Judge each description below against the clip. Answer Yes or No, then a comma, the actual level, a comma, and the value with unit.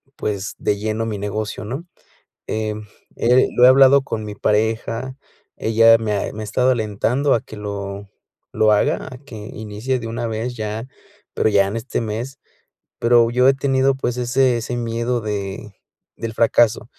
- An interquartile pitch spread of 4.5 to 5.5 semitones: No, average, 2.7 semitones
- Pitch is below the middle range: Yes, low, 115 Hz